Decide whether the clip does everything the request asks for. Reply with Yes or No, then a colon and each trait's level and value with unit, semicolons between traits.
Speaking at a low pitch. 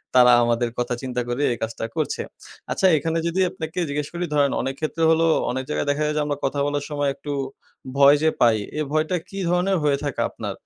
No: medium, 145 Hz